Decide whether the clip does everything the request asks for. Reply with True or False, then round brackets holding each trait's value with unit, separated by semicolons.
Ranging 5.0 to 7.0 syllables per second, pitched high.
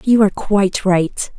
False (4.8 syllables/s; 200 Hz)